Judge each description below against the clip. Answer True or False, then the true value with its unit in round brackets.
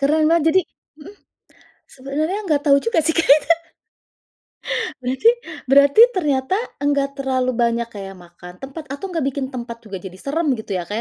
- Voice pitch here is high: True (275 Hz)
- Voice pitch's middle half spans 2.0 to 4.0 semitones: False (4.7 semitones)